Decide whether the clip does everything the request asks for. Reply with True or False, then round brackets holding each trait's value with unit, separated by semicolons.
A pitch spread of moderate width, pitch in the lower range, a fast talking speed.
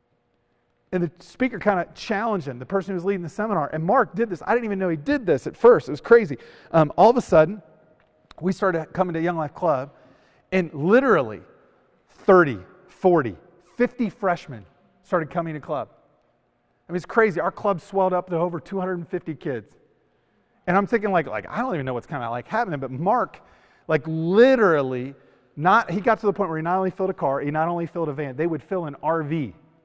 False (4.0 semitones; 180 Hz; 215 wpm)